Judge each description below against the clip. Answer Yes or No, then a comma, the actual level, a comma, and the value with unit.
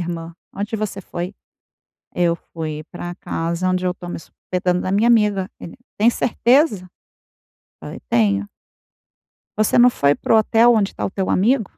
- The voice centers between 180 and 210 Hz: Yes, medium, 185 Hz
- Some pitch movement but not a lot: Yes, average, 3.9 semitones